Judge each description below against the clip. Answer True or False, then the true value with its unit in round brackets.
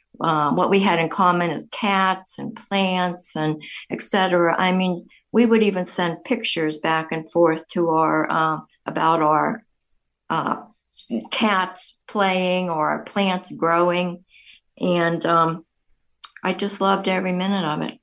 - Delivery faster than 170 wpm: False (145 wpm)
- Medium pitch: True (180 Hz)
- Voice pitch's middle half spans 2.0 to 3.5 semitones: True (2.5 semitones)